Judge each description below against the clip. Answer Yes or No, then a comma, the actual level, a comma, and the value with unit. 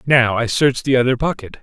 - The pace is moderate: No, fast, 220 wpm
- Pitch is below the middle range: Yes, low, 125 Hz